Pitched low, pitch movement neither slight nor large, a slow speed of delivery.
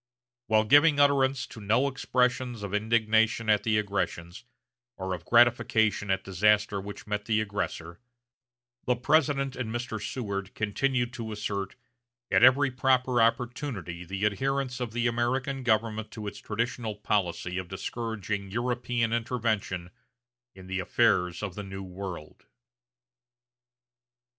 Yes: low, 110 Hz; average, 3.7 semitones; slow, 130 wpm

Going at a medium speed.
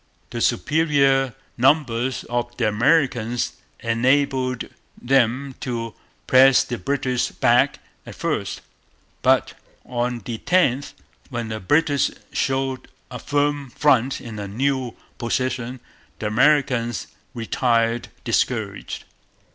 No: slow, 105 wpm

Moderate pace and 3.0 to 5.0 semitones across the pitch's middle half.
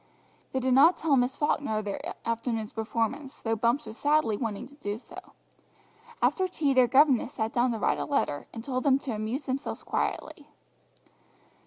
Yes: average, 180 wpm; average, 3.8 semitones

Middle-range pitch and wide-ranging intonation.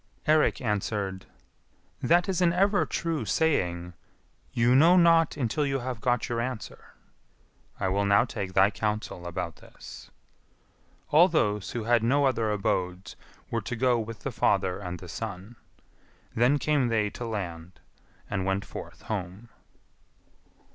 No: low, 110 Hz; wide, 5.9 semitones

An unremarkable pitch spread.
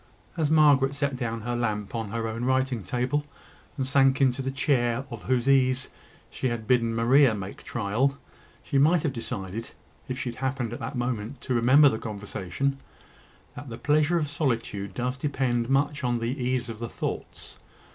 Yes: average, 3.0 semitones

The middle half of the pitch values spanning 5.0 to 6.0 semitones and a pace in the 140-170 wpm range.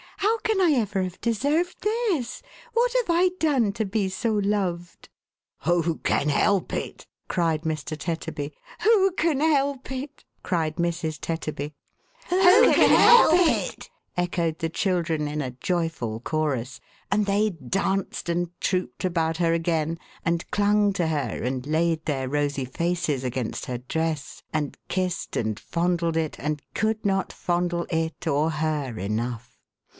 Yes: average, 5.3 semitones; average, 155 wpm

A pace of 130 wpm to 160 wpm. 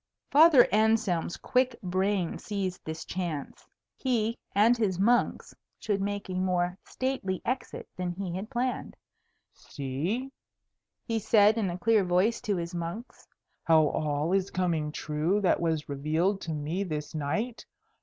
Yes: average, 145 wpm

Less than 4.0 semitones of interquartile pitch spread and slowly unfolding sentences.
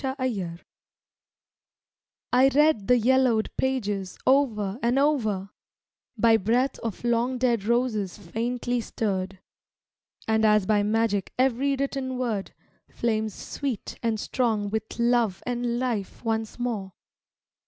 Yes: average, 3.2 semitones; slow, 115 wpm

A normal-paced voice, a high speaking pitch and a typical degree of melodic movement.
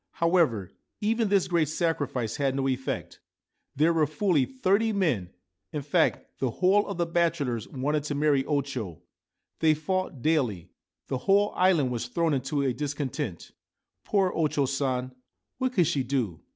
No: average, 160 wpm; medium, 150 Hz; average, 4.8 semitones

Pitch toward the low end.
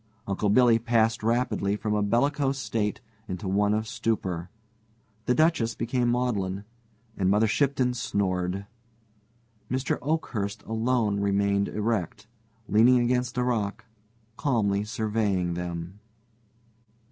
Yes: low, 110 Hz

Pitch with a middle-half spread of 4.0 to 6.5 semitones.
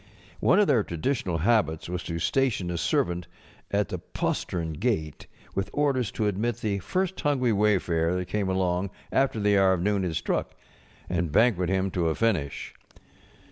Yes: average, 4.5 semitones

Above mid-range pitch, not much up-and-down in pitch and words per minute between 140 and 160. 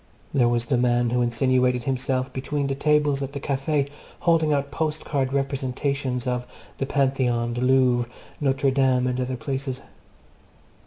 No: low, 130 Hz; narrow, 1.9 semitones; average, 150 wpm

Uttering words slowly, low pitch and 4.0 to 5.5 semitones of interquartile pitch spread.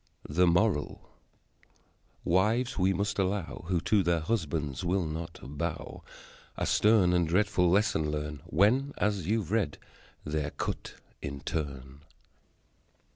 Yes: slow, 125 wpm; very low, 90 Hz; average, 4.9 semitones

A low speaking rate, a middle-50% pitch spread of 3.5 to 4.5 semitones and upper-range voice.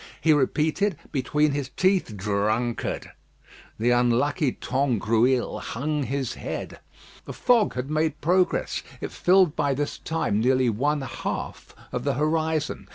No: slow, 130 wpm; average, 4.0 semitones; medium, 140 Hz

